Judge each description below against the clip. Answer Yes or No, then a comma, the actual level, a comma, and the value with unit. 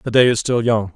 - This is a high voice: No, low, 115 Hz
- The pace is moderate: No, fast, 315 wpm